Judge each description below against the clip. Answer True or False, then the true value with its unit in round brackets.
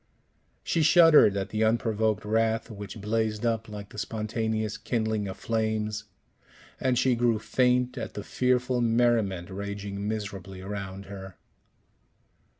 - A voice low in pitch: True (110 Hz)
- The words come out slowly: True (130 wpm)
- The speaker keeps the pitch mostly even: True (2.3 semitones)